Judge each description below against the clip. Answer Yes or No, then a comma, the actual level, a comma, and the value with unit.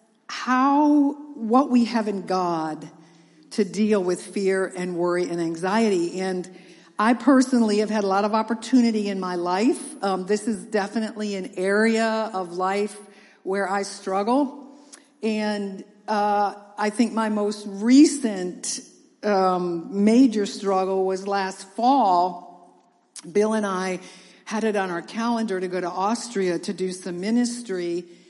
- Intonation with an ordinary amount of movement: Yes, average, 3.3 semitones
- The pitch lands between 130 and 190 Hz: No, high, 205 Hz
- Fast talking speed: No, average, 140 wpm